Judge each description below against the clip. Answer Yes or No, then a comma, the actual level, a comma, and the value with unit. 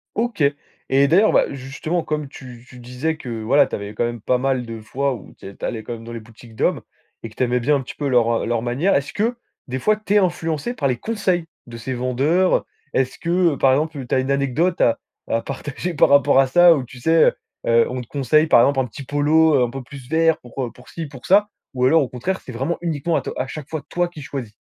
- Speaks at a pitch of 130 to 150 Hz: Yes, low, 135 Hz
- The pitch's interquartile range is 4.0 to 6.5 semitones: Yes, average, 4.6 semitones